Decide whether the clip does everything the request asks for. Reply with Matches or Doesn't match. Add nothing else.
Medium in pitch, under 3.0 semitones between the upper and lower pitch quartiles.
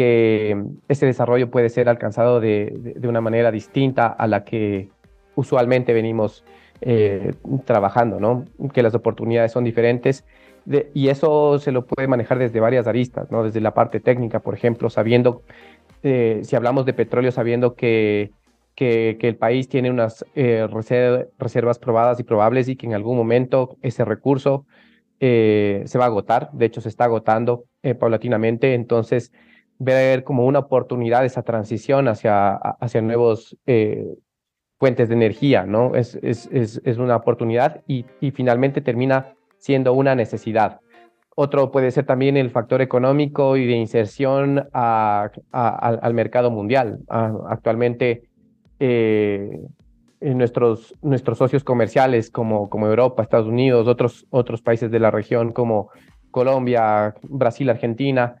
Doesn't match